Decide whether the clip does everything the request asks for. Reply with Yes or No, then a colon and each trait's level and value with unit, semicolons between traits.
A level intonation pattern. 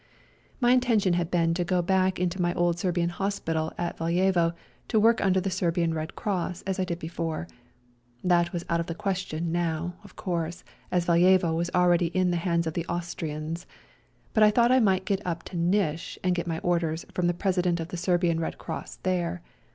Yes: narrow, 1.8 semitones